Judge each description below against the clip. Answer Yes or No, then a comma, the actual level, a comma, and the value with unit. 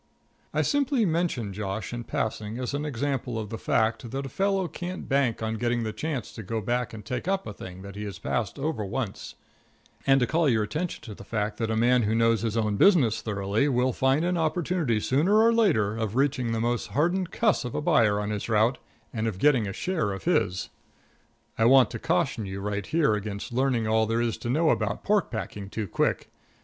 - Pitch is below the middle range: Yes, low, 120 Hz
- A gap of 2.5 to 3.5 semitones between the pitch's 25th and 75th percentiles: No, average, 5.3 semitones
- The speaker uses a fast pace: Yes, fast, 220 wpm